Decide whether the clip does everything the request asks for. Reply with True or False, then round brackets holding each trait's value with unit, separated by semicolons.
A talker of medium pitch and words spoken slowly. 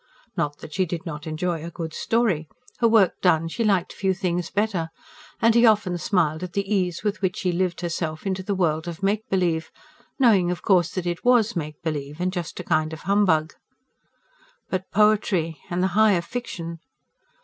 False (180 Hz; 190 wpm)